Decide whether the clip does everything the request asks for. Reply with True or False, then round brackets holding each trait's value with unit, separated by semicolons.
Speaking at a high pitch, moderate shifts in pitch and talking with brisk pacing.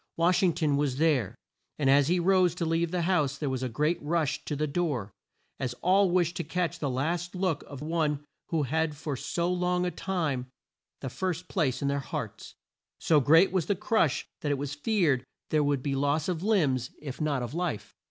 False (155 Hz; 3.9 semitones; 210 wpm)